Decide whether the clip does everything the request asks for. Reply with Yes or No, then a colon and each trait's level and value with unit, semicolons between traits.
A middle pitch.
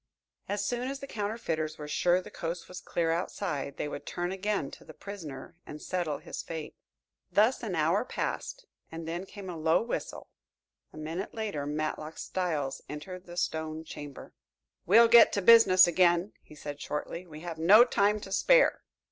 Yes: medium, 175 Hz